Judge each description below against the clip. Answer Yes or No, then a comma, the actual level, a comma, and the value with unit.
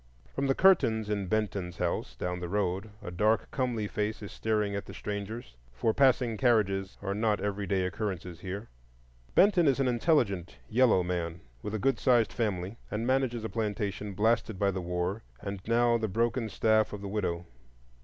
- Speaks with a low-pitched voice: Yes, low, 105 Hz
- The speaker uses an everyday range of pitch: Yes, average, 3.2 semitones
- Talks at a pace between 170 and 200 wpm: Yes, average, 180 wpm